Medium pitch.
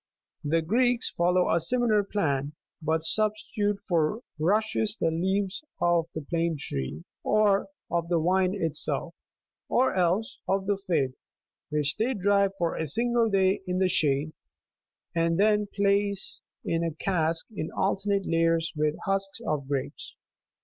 Yes: medium, 180 Hz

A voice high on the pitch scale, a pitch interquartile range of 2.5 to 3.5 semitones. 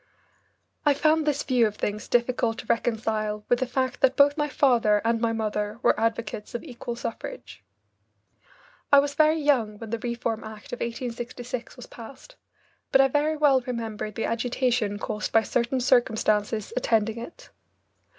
Yes: high, 235 Hz; average, 3.2 semitones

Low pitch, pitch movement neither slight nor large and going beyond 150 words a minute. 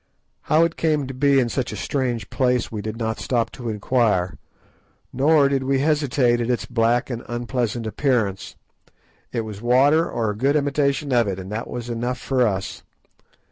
Yes: low, 125 Hz; average, 3.3 semitones; average, 180 wpm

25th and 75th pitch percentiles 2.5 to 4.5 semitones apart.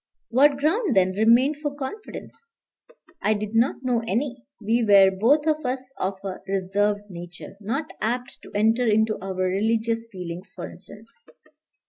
No: average, 4.9 semitones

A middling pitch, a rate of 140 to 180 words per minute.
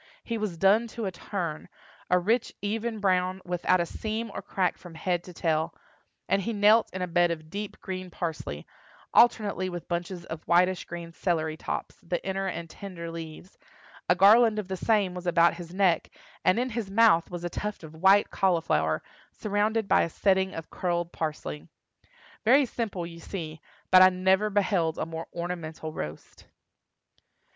Yes: medium, 180 Hz; average, 170 wpm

